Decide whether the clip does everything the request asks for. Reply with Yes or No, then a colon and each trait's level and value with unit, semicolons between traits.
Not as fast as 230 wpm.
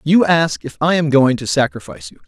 No: fast, 240 wpm